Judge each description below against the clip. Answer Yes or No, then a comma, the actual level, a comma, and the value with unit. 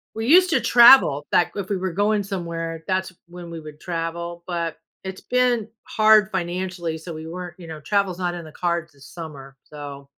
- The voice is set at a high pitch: No, medium, 175 Hz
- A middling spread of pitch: Yes, average, 3.0 semitones